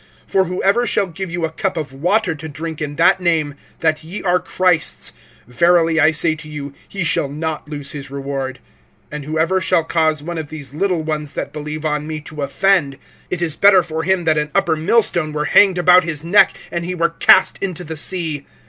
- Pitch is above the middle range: No, medium, 160 Hz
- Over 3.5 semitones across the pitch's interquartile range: No, average, 2.9 semitones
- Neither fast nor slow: No, fast, 210 wpm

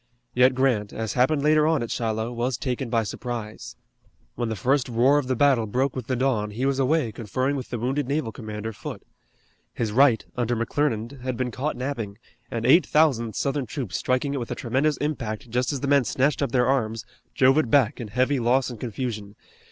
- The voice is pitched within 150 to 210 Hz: No, low, 125 Hz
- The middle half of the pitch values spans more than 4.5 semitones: No, average, 3.3 semitones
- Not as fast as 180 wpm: No, fast, 205 wpm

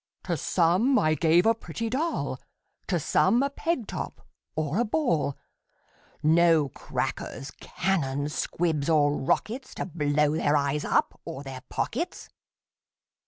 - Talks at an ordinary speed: No, slow, 130 wpm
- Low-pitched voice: No, medium, 165 Hz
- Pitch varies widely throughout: Yes, wide, 7.1 semitones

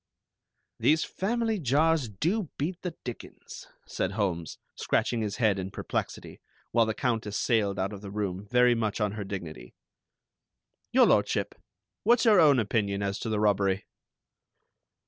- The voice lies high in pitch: No, low, 110 Hz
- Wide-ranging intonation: Yes, wide, 6.4 semitones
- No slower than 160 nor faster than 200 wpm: No, average, 145 wpm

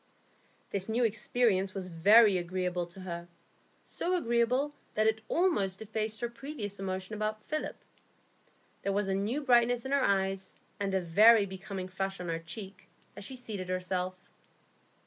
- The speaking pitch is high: Yes, high, 200 Hz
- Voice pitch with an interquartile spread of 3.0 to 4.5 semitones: Yes, average, 3.7 semitones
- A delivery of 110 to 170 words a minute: Yes, average, 155 wpm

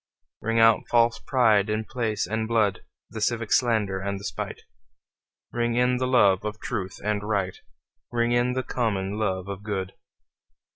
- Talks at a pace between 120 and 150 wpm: No, average, 160 wpm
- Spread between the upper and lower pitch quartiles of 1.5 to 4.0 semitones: Yes, average, 2.9 semitones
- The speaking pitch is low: Yes, low, 110 Hz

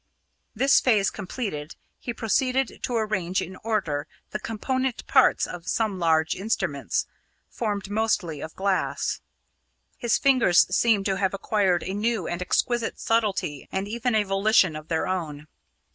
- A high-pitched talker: Yes, high, 200 Hz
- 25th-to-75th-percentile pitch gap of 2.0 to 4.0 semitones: No, average, 4.4 semitones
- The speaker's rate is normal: Yes, average, 145 wpm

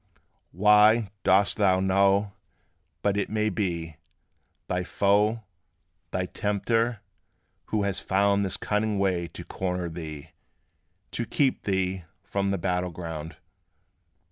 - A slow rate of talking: Yes, slow, 115 wpm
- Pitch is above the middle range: No, low, 100 Hz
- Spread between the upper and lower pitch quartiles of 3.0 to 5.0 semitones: No, narrow, 2.4 semitones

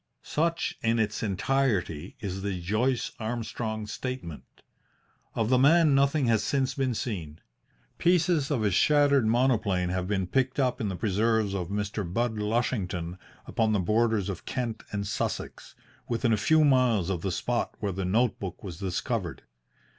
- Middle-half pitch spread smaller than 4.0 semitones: No, average, 4.8 semitones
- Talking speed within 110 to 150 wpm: No, average, 160 wpm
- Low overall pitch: Yes, low, 110 Hz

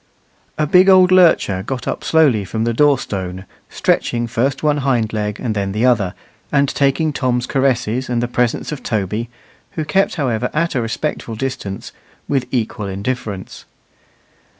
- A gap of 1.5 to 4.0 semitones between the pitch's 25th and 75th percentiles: No, average, 4.5 semitones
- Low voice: Yes, low, 125 Hz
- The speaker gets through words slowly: No, average, 160 wpm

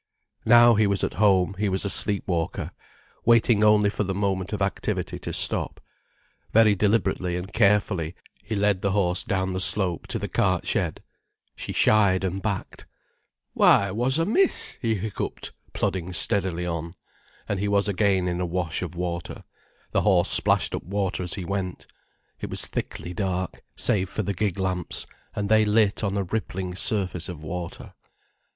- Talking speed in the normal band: Yes, average, 170 wpm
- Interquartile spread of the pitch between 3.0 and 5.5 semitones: No, narrow, 2.4 semitones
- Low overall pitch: Yes, very low, 95 Hz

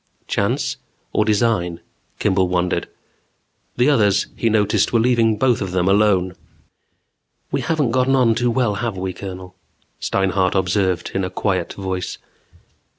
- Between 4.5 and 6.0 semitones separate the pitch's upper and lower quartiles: No, average, 3.8 semitones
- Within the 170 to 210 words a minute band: No, average, 140 wpm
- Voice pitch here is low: Yes, low, 100 Hz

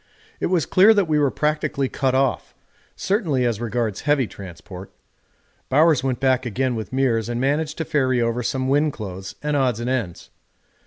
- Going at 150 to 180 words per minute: Yes, average, 175 wpm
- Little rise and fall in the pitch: No, average, 4.0 semitones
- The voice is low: Yes, low, 130 Hz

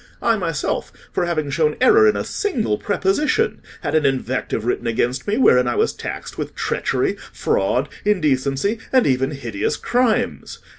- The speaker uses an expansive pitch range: Yes, wide, 8.7 semitones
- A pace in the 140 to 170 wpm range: Yes, average, 155 wpm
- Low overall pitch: No, medium, 150 Hz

